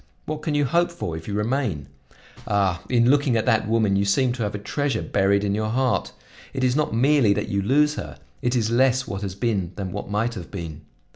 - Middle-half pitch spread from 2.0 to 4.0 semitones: No, average, 4.6 semitones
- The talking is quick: Yes, fast, 230 wpm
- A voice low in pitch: Yes, low, 110 Hz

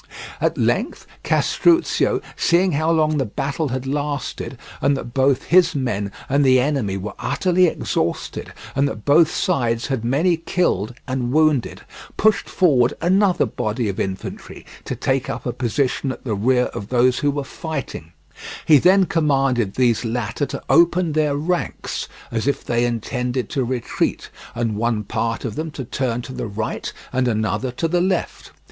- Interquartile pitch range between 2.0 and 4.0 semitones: No, average, 4.9 semitones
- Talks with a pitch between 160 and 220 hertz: No, low, 130 Hz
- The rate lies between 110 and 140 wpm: No, average, 165 wpm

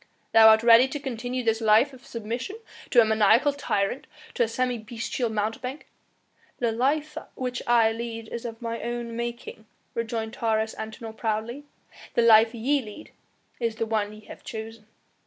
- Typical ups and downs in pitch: No, narrow, 2.0 semitones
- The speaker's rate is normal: Yes, average, 170 wpm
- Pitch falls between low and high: No, high, 230 Hz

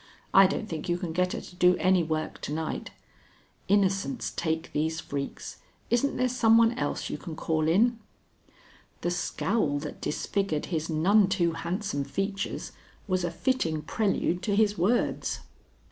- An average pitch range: Yes, average, 4.3 semitones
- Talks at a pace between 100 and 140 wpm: No, average, 160 wpm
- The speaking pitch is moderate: Yes, medium, 180 Hz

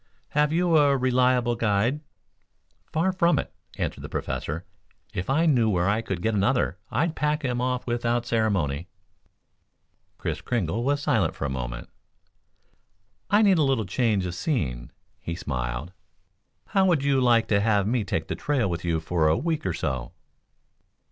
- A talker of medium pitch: No, low, 115 Hz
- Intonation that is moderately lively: No, wide, 8.0 semitones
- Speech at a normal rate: Yes, average, 165 wpm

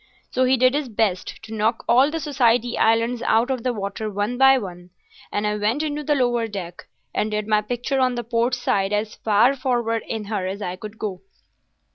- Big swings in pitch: No, average, 3.3 semitones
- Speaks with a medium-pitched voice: No, high, 225 Hz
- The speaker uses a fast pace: Yes, fast, 210 wpm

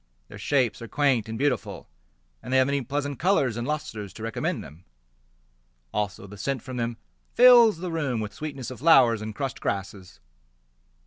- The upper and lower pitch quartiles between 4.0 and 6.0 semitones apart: Yes, average, 4.8 semitones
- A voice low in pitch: Yes, low, 125 Hz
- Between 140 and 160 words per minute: No, average, 175 wpm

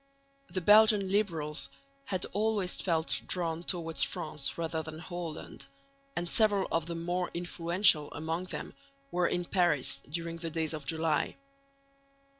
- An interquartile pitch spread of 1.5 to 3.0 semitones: Yes, narrow, 2.4 semitones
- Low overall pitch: No, medium, 170 Hz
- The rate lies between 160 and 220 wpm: No, slow, 135 wpm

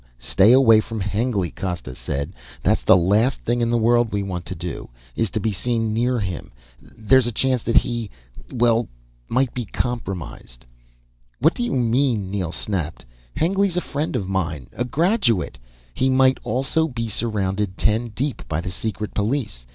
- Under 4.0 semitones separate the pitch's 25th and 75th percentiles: No, average, 4.7 semitones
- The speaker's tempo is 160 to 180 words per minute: Yes, average, 170 wpm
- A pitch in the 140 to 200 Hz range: No, low, 115 Hz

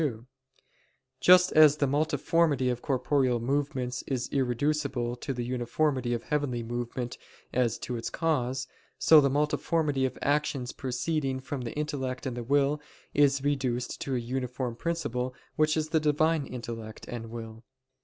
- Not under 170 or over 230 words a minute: No, average, 155 wpm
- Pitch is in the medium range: No, low, 130 Hz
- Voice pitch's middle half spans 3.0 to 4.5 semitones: Yes, average, 3.4 semitones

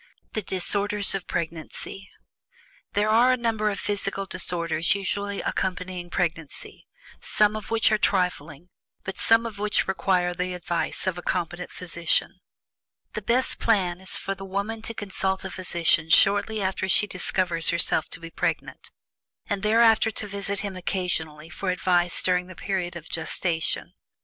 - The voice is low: No, high, 190 Hz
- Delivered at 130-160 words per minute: Yes, average, 155 wpm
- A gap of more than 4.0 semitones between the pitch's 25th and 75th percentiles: No, average, 2.8 semitones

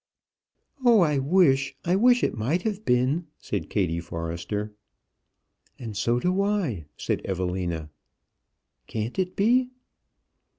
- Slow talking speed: Yes, slow, 120 wpm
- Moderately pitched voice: No, low, 130 Hz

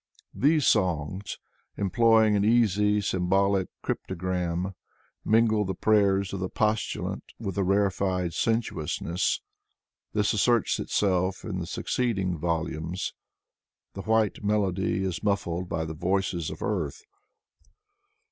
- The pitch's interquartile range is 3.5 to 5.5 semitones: No, average, 2.8 semitones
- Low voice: Yes, very low, 95 Hz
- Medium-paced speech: No, slow, 110 wpm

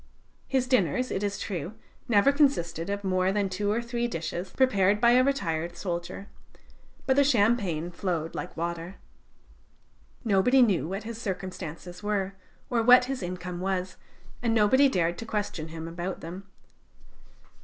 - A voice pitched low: No, high, 195 Hz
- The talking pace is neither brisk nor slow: Yes, average, 150 wpm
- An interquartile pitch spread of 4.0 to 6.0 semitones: Yes, average, 5.2 semitones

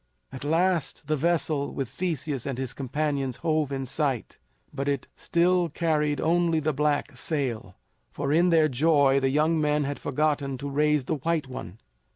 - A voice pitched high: No, medium, 150 Hz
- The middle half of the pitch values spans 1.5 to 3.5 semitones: Yes, narrow, 2.6 semitones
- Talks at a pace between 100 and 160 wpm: No, average, 170 wpm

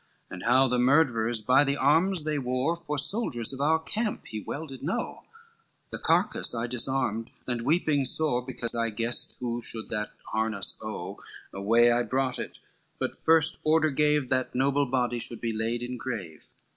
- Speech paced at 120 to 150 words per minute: No, average, 175 wpm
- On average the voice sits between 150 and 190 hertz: No, low, 125 Hz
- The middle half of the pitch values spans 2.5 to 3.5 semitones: No, average, 3.9 semitones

